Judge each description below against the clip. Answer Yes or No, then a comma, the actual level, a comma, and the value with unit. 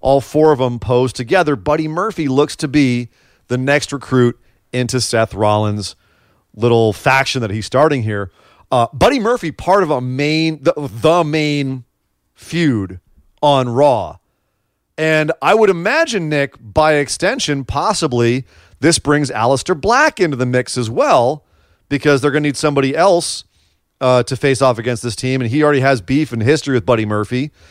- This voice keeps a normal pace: Yes, average, 165 wpm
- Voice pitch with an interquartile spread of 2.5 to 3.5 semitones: No, average, 4.3 semitones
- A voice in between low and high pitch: No, low, 130 Hz